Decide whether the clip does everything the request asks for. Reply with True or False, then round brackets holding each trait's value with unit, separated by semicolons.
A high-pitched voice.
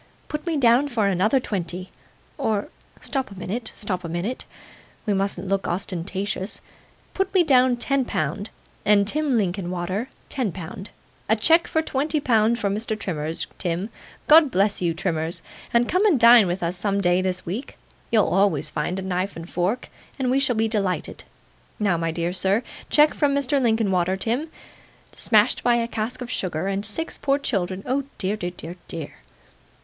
True (205 Hz)